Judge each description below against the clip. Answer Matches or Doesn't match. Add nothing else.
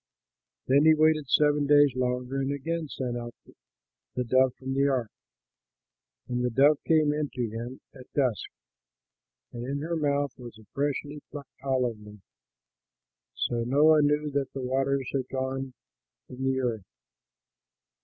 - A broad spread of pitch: Doesn't match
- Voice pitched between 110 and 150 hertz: Matches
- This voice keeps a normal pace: Matches